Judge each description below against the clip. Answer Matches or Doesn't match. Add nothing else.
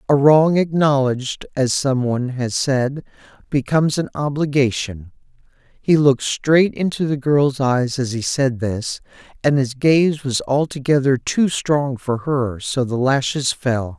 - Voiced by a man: Matches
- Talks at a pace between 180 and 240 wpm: Doesn't match